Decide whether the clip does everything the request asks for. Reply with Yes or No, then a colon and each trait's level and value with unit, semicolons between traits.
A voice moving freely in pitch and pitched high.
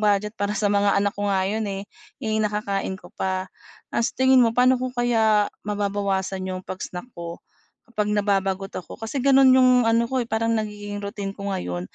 No: narrow, 2.5 semitones; high, 205 Hz